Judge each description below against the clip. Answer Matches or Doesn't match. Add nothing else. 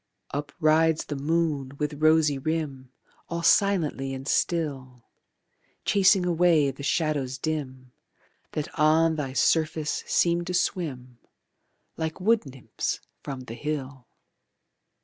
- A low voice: Doesn't match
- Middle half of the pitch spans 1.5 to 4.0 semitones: Matches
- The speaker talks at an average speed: Doesn't match